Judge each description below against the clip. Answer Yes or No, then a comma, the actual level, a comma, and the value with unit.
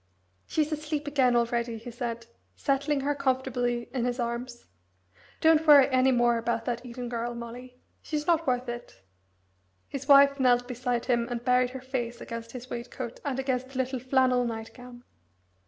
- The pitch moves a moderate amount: No, narrow, 1.9 semitones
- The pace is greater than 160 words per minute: Yes, average, 170 wpm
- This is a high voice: Yes, very high, 250 Hz